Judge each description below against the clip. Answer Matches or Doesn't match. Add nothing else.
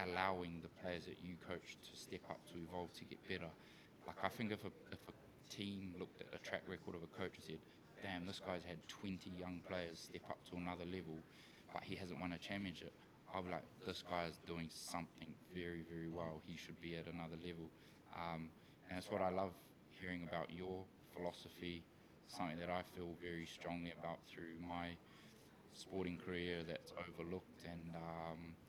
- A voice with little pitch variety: Matches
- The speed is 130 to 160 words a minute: Doesn't match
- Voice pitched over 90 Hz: Doesn't match